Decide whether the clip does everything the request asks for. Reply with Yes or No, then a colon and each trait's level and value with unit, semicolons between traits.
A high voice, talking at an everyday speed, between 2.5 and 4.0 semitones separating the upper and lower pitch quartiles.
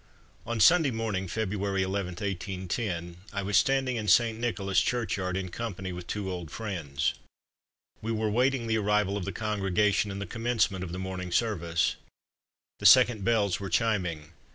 No: low, 100 Hz; average, 160 wpm; average, 3.3 semitones